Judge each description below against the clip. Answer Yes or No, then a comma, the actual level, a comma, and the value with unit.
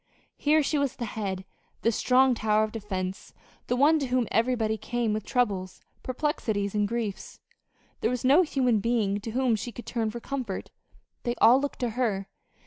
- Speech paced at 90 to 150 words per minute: No, average, 180 wpm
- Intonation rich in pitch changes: No, average, 3.2 semitones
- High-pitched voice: Yes, high, 235 Hz